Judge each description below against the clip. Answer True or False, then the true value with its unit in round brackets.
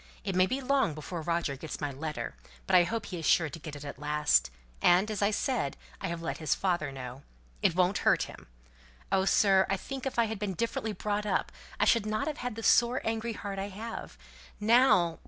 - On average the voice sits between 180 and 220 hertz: True (190 Hz)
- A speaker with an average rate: False (220 wpm)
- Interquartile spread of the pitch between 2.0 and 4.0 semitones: False (5.2 semitones)